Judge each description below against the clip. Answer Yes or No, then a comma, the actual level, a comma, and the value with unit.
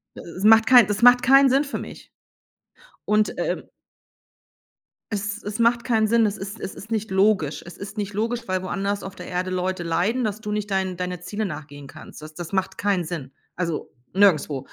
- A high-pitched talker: Yes, high, 200 Hz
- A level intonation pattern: No, average, 3.3 semitones